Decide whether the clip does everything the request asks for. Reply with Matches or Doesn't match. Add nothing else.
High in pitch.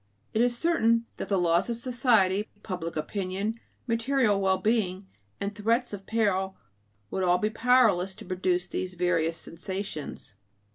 Matches